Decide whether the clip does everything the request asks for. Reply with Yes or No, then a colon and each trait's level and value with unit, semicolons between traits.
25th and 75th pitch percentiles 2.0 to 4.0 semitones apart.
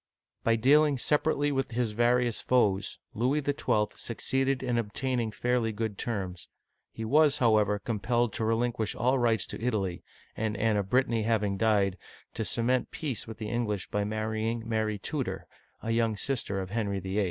Yes: average, 2.8 semitones